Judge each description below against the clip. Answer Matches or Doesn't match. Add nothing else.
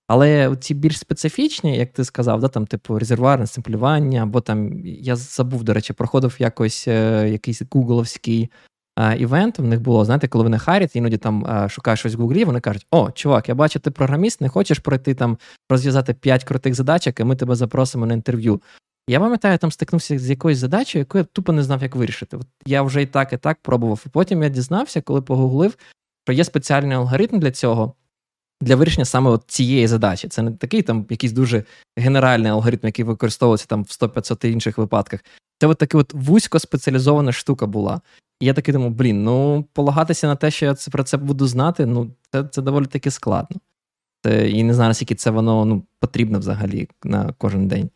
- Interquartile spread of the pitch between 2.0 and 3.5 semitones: Doesn't match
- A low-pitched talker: Matches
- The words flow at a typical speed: Doesn't match